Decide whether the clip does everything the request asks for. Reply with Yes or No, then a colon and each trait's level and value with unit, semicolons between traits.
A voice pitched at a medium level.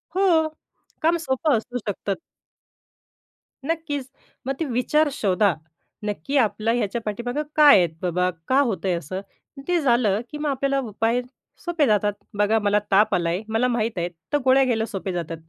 No: high, 235 Hz